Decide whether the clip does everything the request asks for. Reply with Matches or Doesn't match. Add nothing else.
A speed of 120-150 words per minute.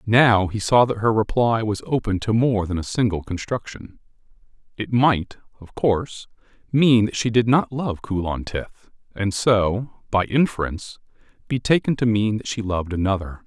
Doesn't match